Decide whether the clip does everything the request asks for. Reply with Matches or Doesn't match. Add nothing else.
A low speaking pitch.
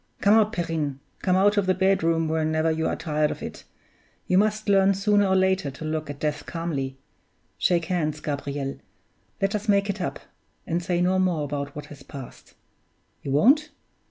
Doesn't match